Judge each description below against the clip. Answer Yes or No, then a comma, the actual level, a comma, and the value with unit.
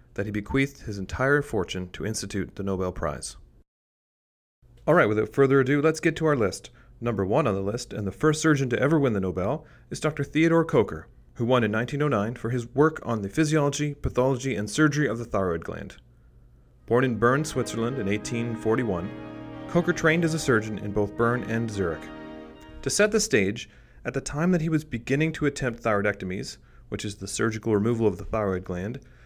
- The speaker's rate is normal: Yes, average, 195 wpm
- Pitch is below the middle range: Yes, low, 115 Hz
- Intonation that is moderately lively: No, wide, 6.3 semitones